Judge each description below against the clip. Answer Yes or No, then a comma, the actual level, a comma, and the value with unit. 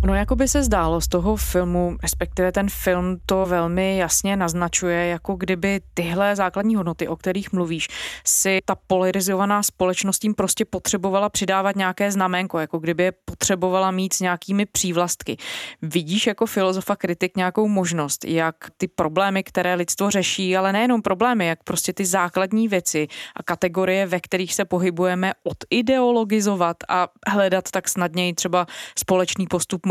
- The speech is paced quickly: No, average, 150 wpm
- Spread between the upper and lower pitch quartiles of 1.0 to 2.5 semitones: Yes, narrow, 1.8 semitones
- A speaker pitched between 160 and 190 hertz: Yes, medium, 185 Hz